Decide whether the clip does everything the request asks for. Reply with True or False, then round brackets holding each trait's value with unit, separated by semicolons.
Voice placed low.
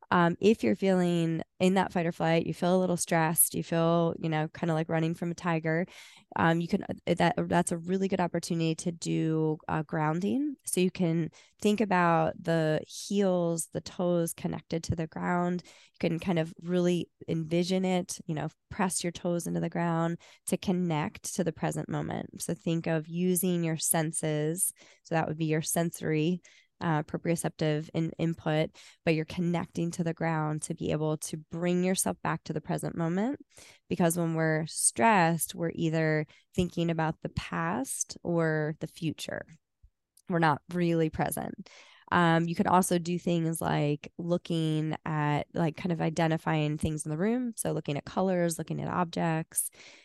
False (170 Hz)